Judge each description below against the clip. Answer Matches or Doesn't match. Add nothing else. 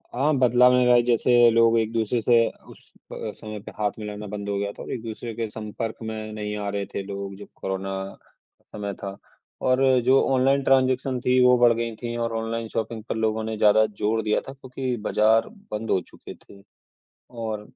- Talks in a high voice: Doesn't match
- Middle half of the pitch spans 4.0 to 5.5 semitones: Doesn't match